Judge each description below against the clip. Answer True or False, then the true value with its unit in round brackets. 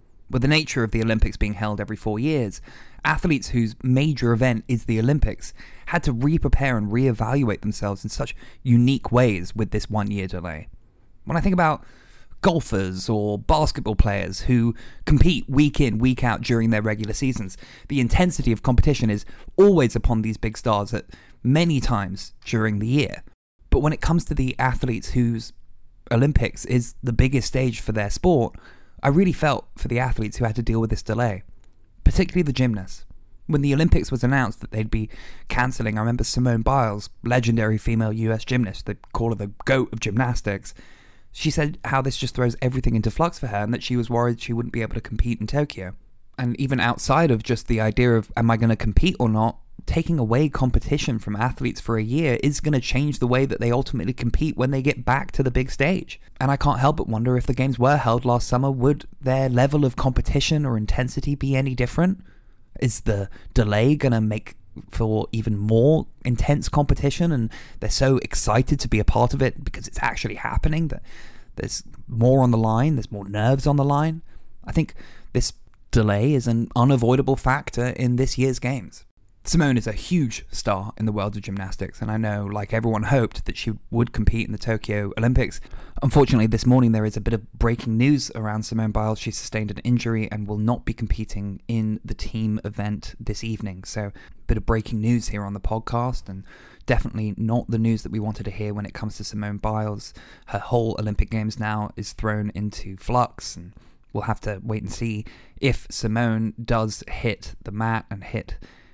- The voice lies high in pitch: False (115 Hz)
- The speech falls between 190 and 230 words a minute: True (200 wpm)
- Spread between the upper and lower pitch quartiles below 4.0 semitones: True (3.5 semitones)